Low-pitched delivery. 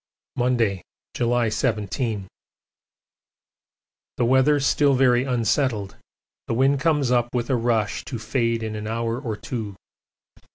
Yes: low, 120 Hz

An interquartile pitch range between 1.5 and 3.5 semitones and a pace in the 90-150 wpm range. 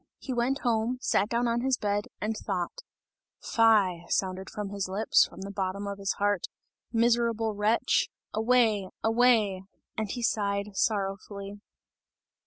Yes: average, 2.7 semitones; average, 140 wpm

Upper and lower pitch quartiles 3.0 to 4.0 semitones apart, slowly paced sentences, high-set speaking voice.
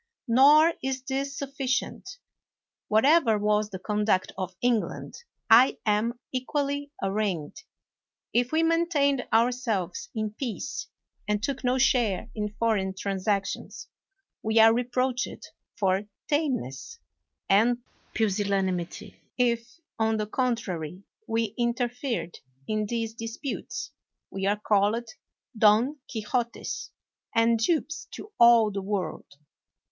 Yes: average, 3.7 semitones; slow, 110 wpm; high, 230 Hz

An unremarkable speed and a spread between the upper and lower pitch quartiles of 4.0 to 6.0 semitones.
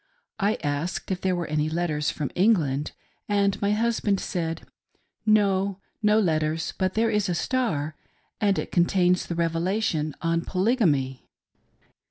Yes: average, 155 wpm; average, 4.5 semitones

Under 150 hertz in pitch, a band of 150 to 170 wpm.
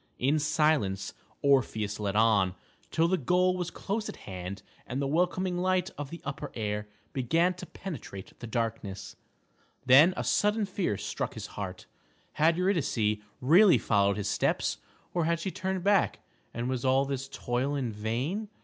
Yes: medium, 140 Hz; average, 160 wpm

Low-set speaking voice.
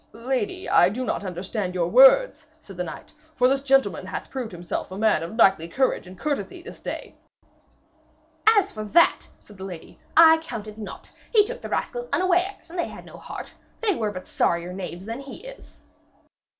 No: high, 230 Hz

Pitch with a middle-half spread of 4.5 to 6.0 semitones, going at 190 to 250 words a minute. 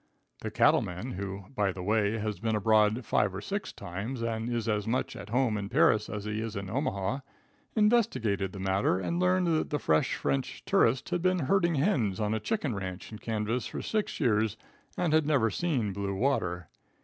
Yes: wide, 5.5 semitones; average, 195 wpm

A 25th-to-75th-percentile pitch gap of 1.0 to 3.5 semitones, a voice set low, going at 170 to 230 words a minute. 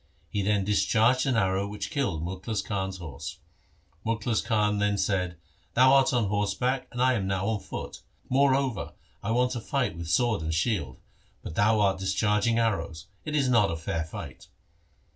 No: average, 4.2 semitones; low, 105 Hz; average, 180 wpm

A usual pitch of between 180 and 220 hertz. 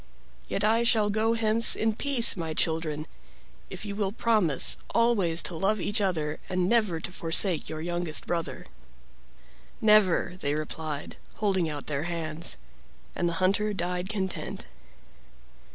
Yes: medium, 185 Hz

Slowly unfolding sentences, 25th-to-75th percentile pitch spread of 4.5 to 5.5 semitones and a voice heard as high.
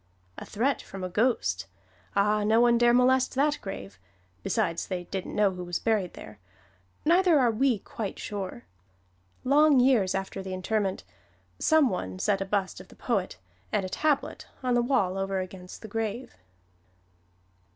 No: average, 160 wpm; average, 4.9 semitones; high, 205 Hz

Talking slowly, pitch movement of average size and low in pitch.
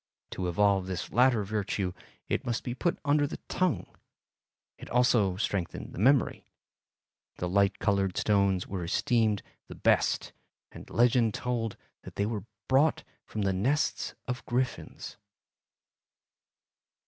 Yes: slow, 130 wpm; average, 4.3 semitones; low, 105 Hz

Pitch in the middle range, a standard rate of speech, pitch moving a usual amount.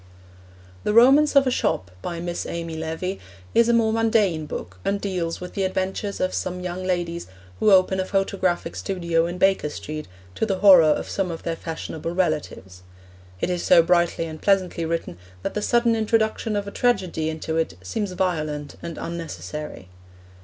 Yes: medium, 180 Hz; average, 175 wpm; average, 3.4 semitones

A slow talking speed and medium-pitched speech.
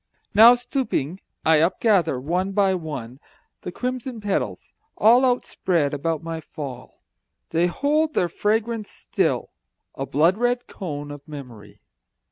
Yes: slow, 125 wpm; medium, 175 Hz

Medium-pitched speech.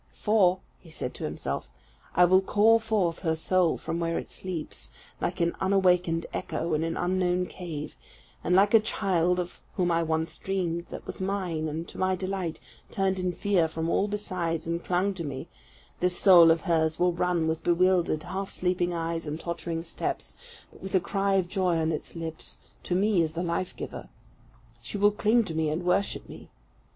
Yes: medium, 175 Hz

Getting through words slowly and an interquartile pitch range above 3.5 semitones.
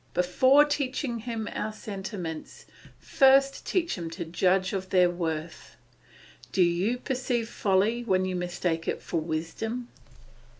Yes: slow, 130 wpm; wide, 5.5 semitones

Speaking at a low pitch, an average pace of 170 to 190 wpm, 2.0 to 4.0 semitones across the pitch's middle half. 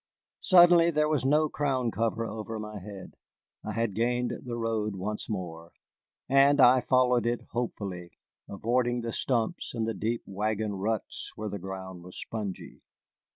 No: low, 115 Hz; average, 155 wpm; average, 3.5 semitones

